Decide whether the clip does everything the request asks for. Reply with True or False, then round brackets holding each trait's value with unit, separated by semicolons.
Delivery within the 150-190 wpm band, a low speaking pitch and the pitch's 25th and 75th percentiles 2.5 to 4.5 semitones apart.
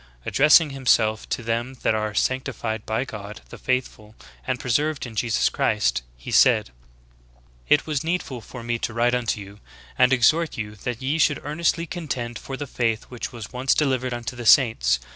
True (180 wpm; 120 Hz; 3.4 semitones)